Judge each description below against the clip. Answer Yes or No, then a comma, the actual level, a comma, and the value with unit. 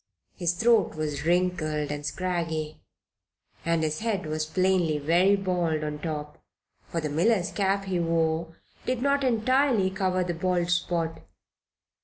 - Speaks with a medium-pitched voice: Yes, medium, 175 Hz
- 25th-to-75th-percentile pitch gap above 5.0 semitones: No, average, 3.3 semitones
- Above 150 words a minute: No, average, 140 wpm